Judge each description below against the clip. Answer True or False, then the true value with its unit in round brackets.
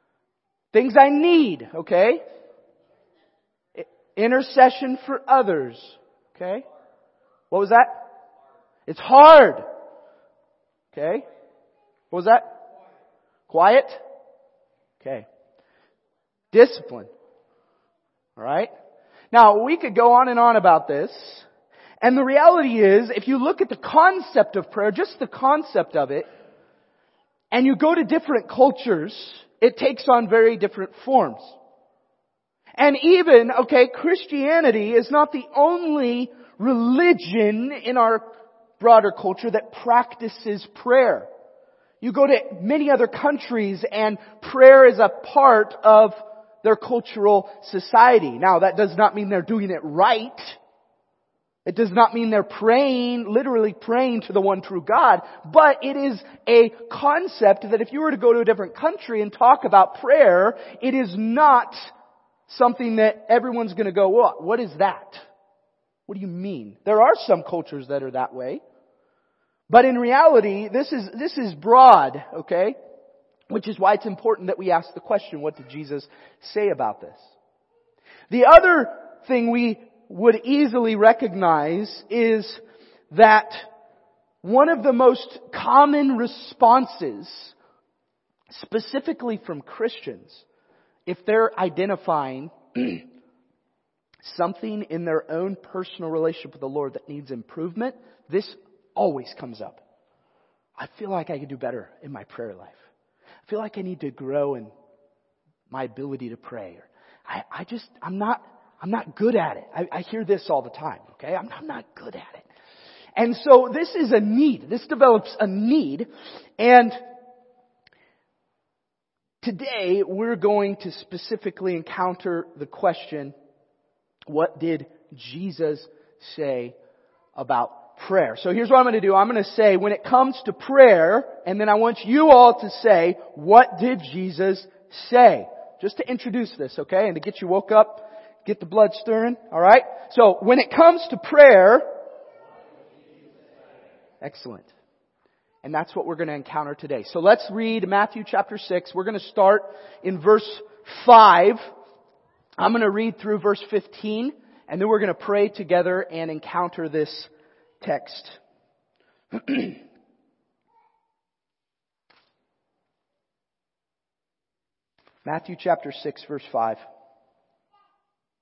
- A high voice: True (225 Hz)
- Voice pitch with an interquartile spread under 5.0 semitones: False (5.5 semitones)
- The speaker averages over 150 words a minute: False (135 wpm)